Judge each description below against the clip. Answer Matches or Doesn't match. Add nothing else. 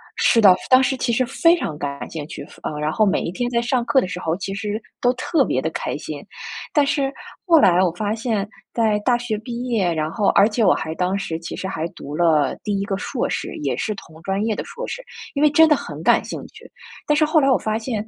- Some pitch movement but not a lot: Doesn't match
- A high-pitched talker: Matches